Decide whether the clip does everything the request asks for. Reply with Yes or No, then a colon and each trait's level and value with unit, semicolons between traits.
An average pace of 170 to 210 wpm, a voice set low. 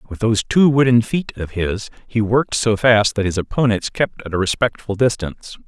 Yes: average, 200 wpm; low, 110 Hz